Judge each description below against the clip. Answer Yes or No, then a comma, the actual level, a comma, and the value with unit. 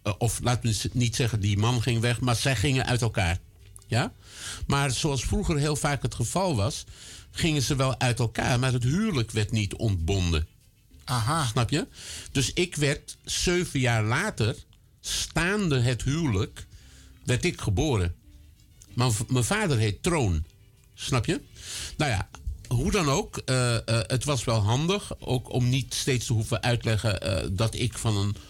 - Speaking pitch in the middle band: No, low, 120 Hz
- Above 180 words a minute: No, average, 170 wpm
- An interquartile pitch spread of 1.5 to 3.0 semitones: No, average, 4.2 semitones